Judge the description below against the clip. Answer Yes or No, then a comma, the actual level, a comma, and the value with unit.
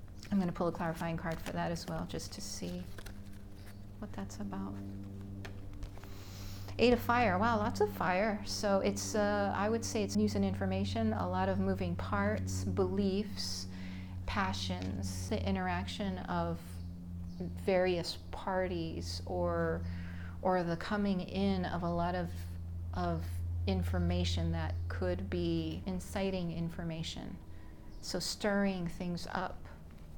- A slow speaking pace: Yes, slow, 130 wpm